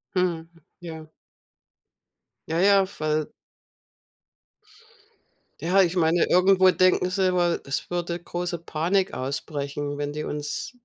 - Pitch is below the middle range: No, medium, 170 Hz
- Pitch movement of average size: Yes, average, 3.1 semitones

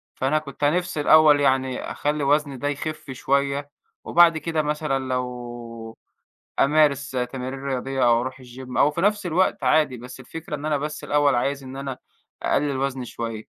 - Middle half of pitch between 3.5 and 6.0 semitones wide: No, average, 2.7 semitones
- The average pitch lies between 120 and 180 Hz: Yes, medium, 140 Hz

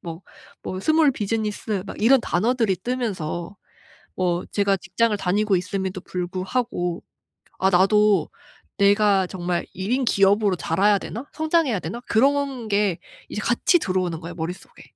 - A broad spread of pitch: No, average, 4.0 semitones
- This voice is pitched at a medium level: No, high, 200 Hz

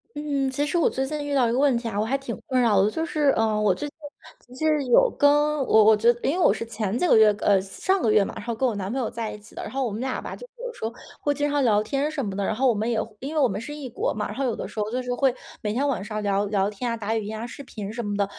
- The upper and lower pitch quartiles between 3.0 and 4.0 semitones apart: No, average, 4.7 semitones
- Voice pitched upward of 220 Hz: Yes, high, 235 Hz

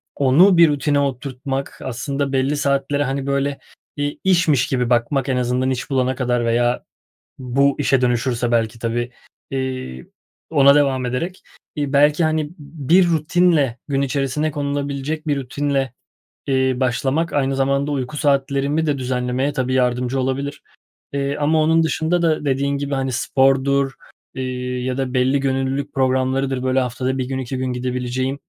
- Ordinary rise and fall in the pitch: No, narrow, 2.0 semitones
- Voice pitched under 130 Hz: No, low, 135 Hz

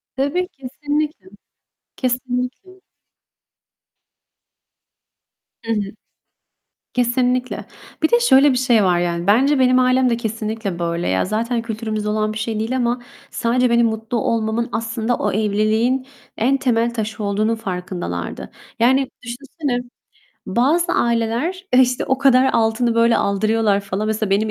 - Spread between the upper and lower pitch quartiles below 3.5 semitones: Yes, average, 3.0 semitones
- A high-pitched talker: Yes, high, 230 Hz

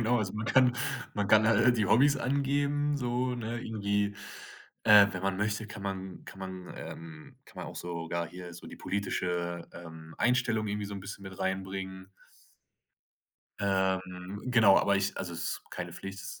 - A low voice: Yes, low, 100 Hz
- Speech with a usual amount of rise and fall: Yes, average, 3.3 semitones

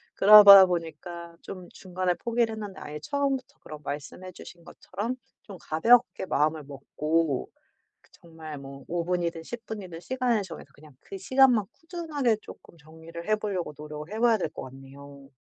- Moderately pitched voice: Yes, medium, 175 Hz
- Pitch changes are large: Yes, wide, 5.8 semitones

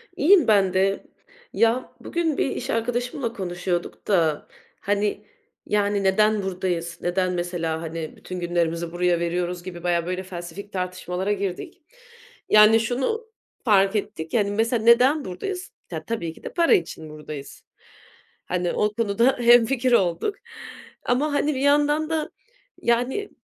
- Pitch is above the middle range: Yes, high, 200 Hz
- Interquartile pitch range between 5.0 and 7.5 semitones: Yes, wide, 5.6 semitones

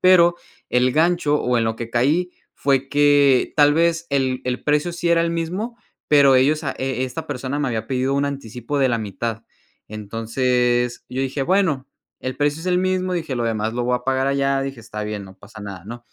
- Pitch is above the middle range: No, low, 135 Hz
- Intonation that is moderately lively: Yes, average, 3.8 semitones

